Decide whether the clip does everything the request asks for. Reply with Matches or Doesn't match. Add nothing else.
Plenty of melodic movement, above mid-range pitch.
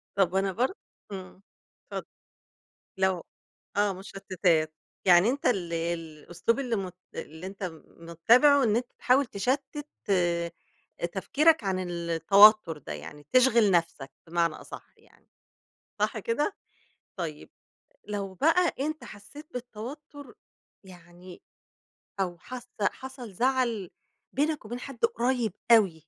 Matches